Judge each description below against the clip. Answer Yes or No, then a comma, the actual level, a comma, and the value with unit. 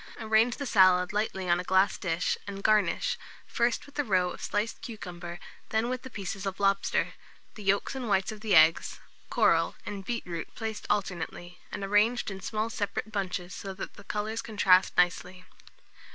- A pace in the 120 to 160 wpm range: No, average, 175 wpm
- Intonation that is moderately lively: Yes, average, 3.1 semitones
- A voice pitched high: Yes, high, 200 Hz